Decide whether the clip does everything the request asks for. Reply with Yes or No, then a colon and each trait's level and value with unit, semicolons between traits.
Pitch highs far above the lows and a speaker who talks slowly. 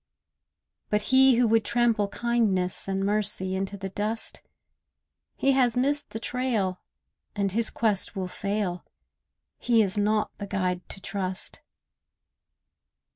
No: average, 3.3 semitones; slow, 130 wpm